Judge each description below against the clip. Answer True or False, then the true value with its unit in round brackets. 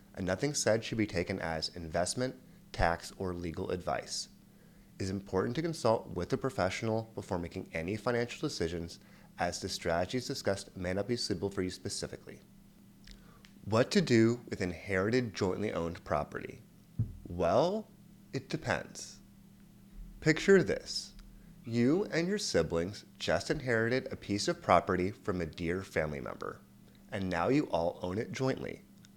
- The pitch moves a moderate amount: False (6.0 semitones)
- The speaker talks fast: False (145 wpm)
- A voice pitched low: True (100 Hz)